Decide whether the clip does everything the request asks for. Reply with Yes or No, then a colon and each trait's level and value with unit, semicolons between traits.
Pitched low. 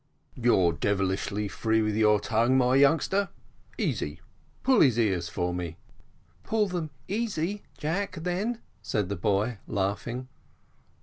Yes: low, 120 Hz